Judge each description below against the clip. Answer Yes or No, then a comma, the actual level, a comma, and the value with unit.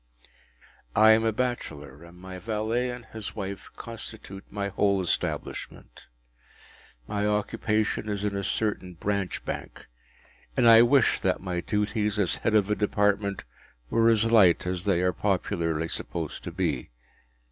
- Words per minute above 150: No, average, 145 wpm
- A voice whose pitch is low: Yes, low, 105 Hz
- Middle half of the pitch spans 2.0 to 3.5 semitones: Yes, average, 2.9 semitones